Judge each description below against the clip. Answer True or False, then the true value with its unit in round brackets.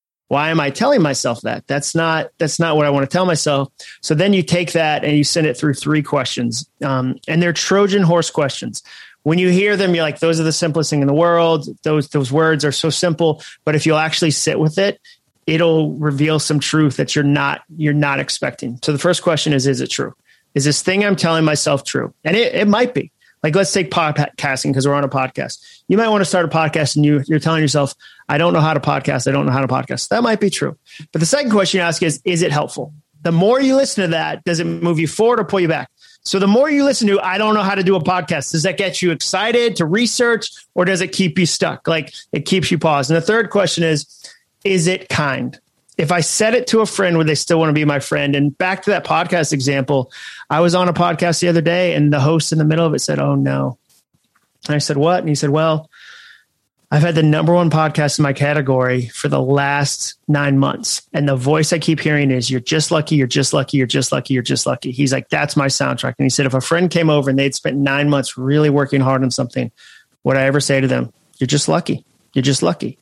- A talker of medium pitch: True (155 Hz)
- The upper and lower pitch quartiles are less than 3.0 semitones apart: False (3.6 semitones)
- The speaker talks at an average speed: False (255 wpm)